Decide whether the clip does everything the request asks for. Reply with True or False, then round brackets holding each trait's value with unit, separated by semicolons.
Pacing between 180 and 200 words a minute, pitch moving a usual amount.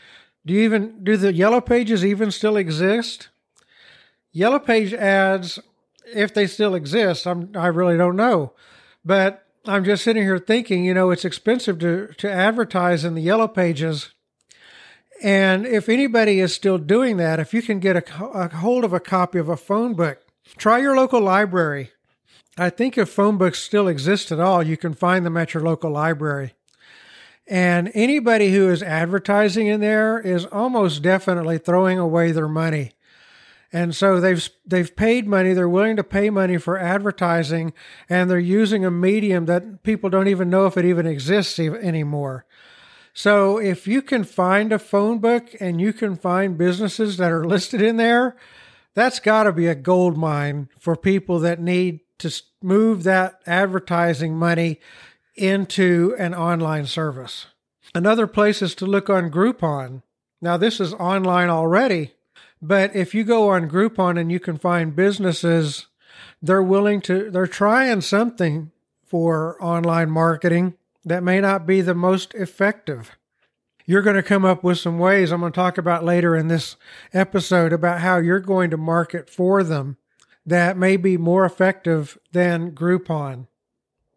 False (165 wpm; 3.2 semitones)